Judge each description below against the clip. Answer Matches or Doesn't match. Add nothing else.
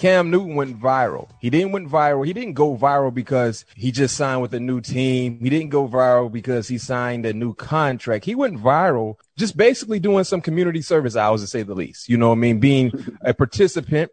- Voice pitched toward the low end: Matches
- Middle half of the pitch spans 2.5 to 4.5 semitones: Doesn't match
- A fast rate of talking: Matches